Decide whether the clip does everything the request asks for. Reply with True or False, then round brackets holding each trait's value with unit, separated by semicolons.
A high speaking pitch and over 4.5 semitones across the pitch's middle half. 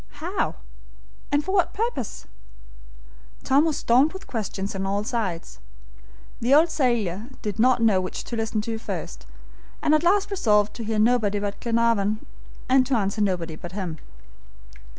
True (225 Hz; 5.2 semitones)